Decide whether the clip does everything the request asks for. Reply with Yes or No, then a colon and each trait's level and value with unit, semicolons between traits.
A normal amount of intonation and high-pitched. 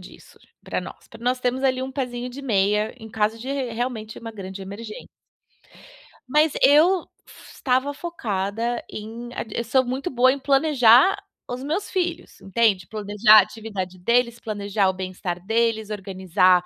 Yes: average, 4.0 semitones; high, 230 Hz